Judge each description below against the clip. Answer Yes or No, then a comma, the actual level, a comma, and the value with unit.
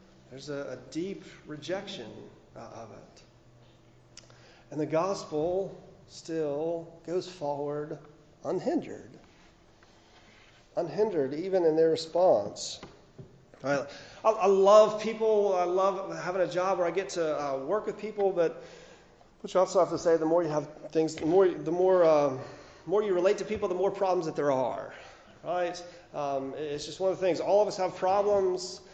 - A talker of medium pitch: Yes, medium, 175 Hz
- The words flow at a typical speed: Yes, average, 160 wpm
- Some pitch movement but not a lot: Yes, average, 4.2 semitones